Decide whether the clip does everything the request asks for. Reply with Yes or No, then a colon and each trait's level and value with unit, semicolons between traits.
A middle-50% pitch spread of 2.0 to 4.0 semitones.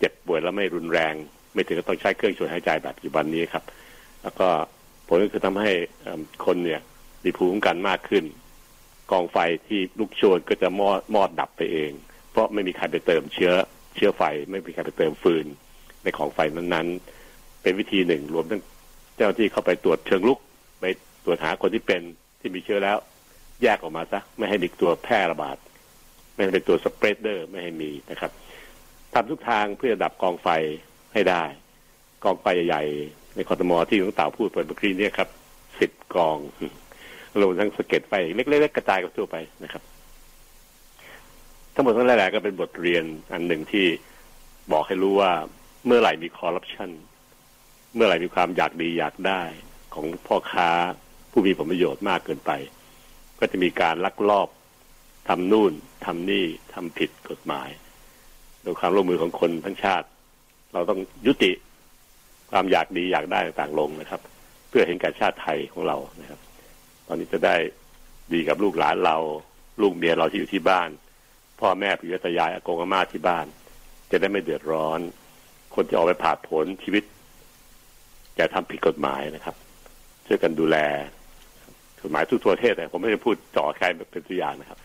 Yes: average, 3.5 semitones